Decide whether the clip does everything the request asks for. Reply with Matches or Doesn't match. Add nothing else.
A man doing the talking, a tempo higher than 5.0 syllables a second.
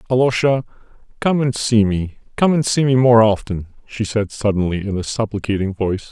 Matches